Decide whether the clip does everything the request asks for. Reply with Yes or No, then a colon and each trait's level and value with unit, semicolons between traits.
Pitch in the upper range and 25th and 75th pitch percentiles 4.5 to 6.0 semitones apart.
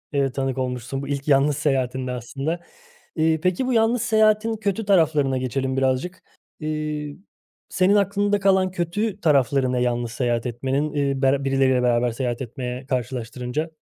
No: medium, 140 Hz; wide, 5.5 semitones